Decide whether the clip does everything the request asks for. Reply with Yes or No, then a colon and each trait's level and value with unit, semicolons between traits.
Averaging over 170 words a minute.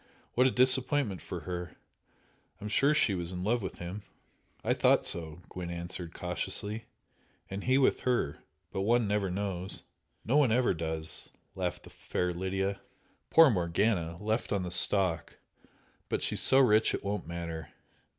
No: average, 160 wpm